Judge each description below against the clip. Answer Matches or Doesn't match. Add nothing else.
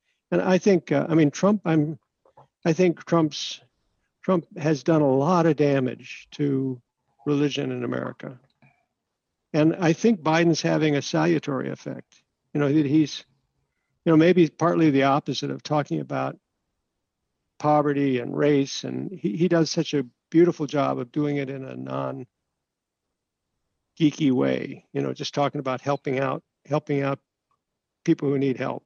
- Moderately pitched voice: Matches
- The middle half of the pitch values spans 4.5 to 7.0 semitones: Doesn't match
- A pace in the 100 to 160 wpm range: Matches